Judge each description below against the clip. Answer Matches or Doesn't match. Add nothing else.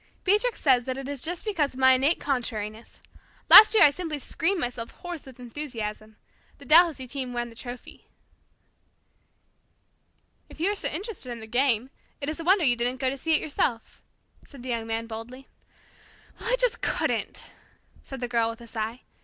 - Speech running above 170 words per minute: Matches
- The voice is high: Matches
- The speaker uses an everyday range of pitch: Matches